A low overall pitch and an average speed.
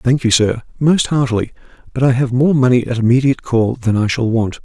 No: low, 125 Hz; fast, 220 wpm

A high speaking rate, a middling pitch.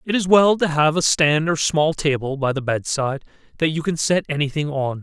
Yes: fast, 250 wpm; medium, 150 Hz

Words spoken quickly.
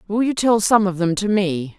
Yes: fast, 270 wpm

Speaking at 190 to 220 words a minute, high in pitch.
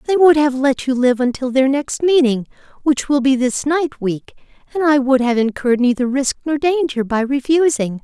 Yes: average, 200 wpm; very high, 270 Hz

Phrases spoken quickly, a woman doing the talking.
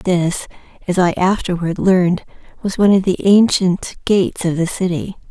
No: average, 160 wpm; female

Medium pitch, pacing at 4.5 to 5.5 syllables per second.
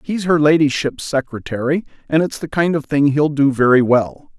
Yes: medium, 145 Hz; 5.0 syllables/s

